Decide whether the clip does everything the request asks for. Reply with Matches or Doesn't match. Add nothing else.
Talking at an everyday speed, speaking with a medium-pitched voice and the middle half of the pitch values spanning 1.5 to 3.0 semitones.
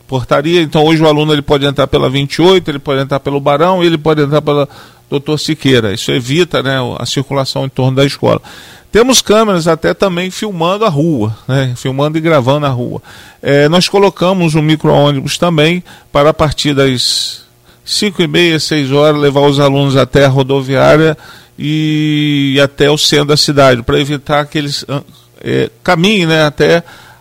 Matches